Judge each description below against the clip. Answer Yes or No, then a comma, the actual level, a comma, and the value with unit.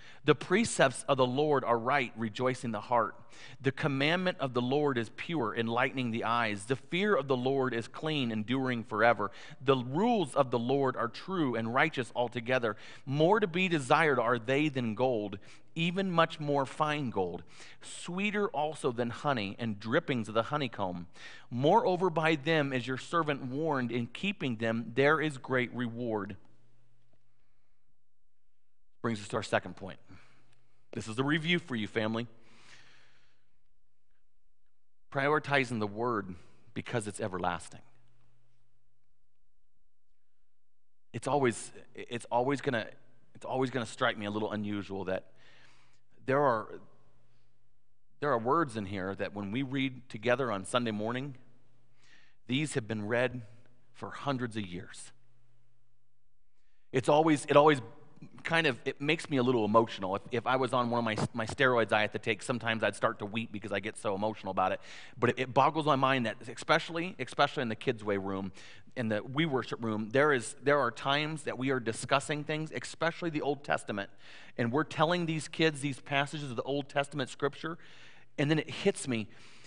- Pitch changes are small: No, average, 3.6 semitones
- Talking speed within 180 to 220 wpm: No, average, 165 wpm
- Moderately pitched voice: No, low, 125 Hz